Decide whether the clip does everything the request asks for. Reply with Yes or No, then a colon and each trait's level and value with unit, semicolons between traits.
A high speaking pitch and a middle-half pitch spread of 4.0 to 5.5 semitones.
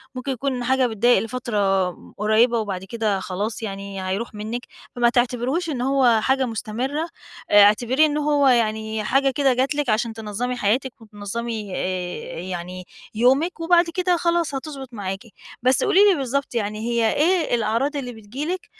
Yes: high, 240 Hz; average, 4.4 semitones